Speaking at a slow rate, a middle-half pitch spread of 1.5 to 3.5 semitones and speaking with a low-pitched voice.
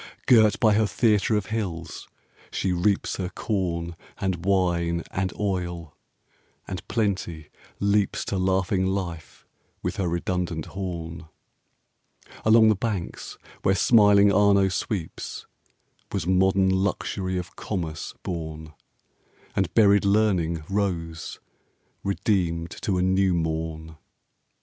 Yes: slow, 115 wpm; average, 3.0 semitones; very low, 95 Hz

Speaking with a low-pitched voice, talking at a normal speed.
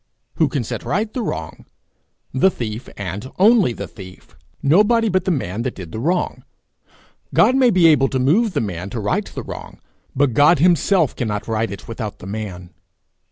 Yes: low, 130 Hz; average, 185 wpm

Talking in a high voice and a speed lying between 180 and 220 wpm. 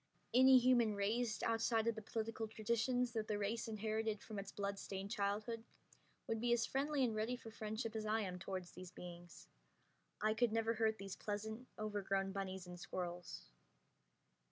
No: high, 215 Hz; average, 165 wpm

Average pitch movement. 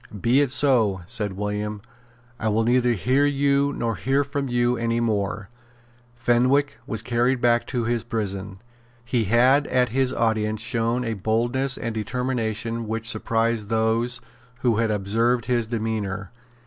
No: narrow, 2.3 semitones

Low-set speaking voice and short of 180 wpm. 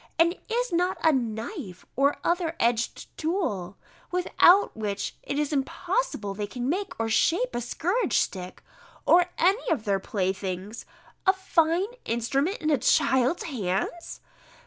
No: very high, 280 Hz; average, 140 wpm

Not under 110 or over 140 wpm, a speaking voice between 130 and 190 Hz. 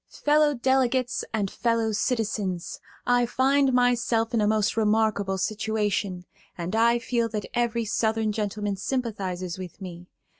No: slow, 135 wpm; high, 220 Hz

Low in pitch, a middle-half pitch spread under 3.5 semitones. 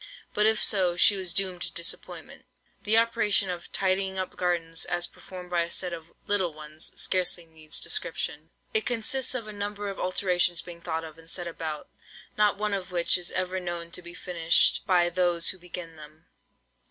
No: medium, 180 Hz; narrow, 2.5 semitones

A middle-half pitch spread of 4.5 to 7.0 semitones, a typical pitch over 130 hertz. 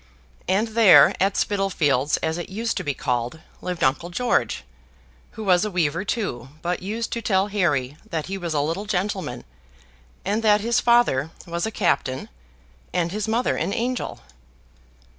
Yes: average, 4.9 semitones; high, 190 Hz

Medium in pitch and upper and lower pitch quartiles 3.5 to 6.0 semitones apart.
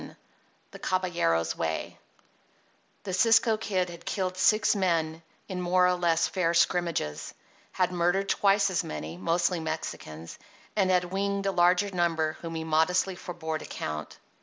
No: medium, 180 Hz; average, 2.7 semitones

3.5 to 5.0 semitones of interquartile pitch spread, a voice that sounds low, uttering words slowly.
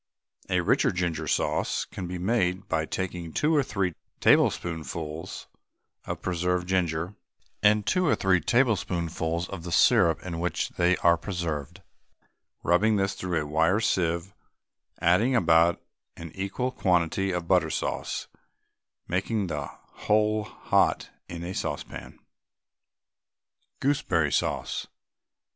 No: average, 3.0 semitones; very low, 90 Hz; slow, 120 wpm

